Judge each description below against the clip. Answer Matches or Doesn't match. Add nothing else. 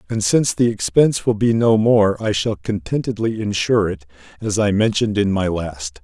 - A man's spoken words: Matches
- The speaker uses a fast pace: Doesn't match